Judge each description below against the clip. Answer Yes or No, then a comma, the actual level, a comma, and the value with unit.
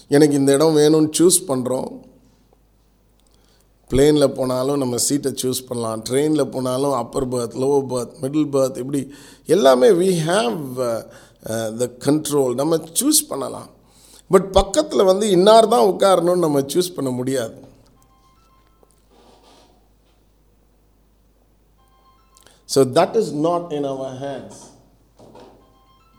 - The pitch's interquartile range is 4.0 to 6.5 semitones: No, average, 3.6 semitones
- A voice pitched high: No, medium, 140 Hz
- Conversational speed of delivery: Yes, average, 105 wpm